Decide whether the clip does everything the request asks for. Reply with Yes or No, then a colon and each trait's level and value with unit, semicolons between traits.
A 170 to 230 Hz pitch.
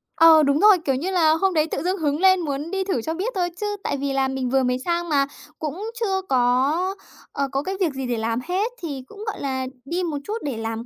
No: very high, 310 Hz